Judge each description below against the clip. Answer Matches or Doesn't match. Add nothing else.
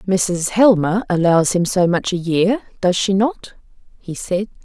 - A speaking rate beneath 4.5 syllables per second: Matches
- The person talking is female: Matches